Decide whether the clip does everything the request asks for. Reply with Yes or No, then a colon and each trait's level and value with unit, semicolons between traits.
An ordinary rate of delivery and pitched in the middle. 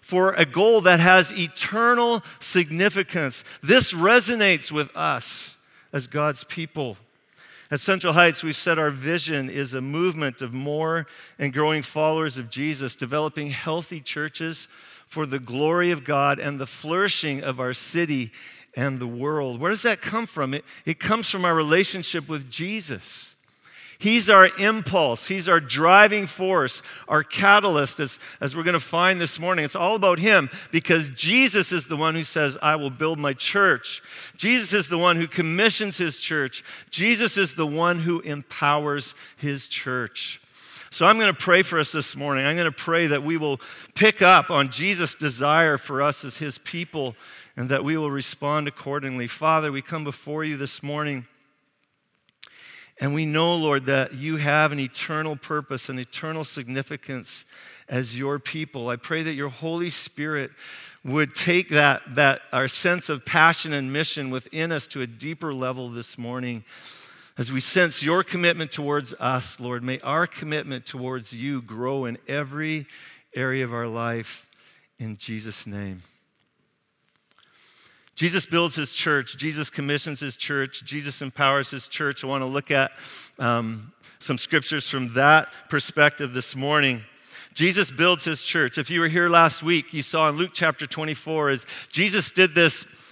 Yes: average, 165 wpm; medium, 150 Hz